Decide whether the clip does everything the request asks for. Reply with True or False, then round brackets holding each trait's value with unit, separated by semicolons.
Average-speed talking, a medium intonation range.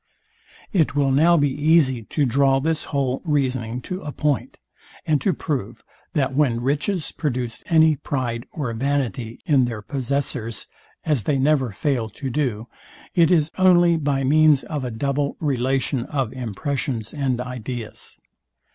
True (145 wpm; 3.3 semitones)